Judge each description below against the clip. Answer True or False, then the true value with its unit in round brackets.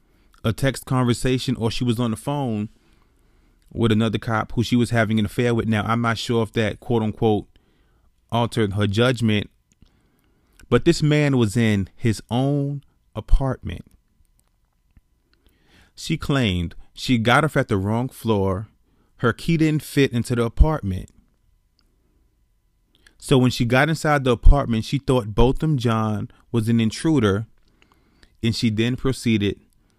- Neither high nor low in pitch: False (115 Hz)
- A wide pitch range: False (3.4 semitones)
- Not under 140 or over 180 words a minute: True (145 wpm)